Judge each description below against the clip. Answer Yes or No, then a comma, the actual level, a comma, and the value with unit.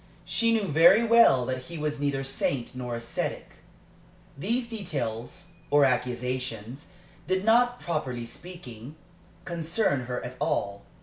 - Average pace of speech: No, slow, 125 wpm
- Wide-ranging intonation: Yes, wide, 6.6 semitones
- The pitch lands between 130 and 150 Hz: Yes, medium, 140 Hz